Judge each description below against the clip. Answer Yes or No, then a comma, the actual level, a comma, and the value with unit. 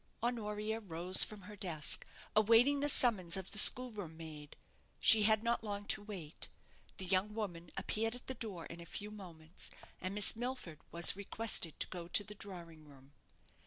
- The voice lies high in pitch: Yes, high, 200 Hz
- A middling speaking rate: Yes, average, 175 wpm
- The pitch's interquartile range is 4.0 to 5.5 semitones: Yes, average, 4.3 semitones